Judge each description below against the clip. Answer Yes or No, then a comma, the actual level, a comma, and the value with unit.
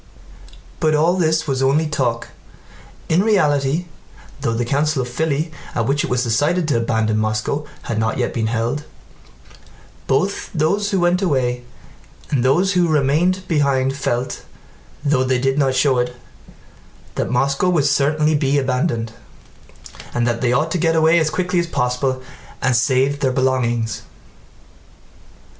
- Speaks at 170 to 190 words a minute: No, average, 150 wpm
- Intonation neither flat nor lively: Yes, average, 4.2 semitones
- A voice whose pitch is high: No, medium, 140 Hz